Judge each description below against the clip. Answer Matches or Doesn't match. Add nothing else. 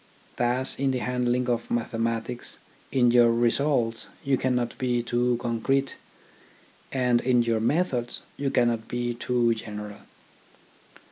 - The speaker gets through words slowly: Matches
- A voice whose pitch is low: Matches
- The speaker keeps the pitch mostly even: Matches